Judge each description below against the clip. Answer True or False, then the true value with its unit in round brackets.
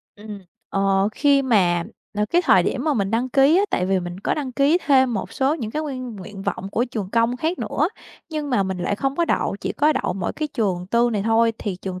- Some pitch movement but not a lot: False (6.1 semitones)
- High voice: True (230 Hz)